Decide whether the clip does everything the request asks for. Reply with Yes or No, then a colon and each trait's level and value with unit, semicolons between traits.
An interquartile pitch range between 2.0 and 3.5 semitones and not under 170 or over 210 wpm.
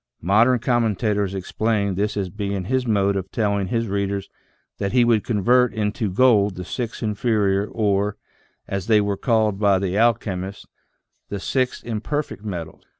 No: average, 2.7 semitones; average, 155 wpm